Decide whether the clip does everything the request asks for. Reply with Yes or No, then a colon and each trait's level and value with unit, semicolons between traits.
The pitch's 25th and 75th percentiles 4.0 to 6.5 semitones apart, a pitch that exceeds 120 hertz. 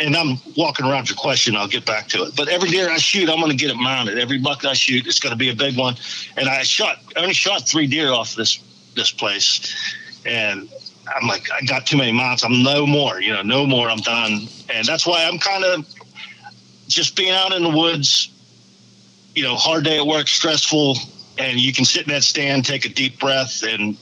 Yes: average, 4.4 semitones; low, 135 Hz